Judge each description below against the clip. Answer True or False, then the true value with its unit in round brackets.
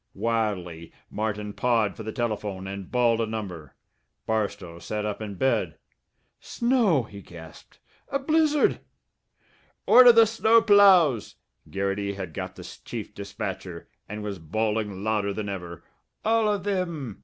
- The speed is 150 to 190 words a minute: False (135 wpm)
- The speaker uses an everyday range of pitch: False (9.0 semitones)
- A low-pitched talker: True (110 Hz)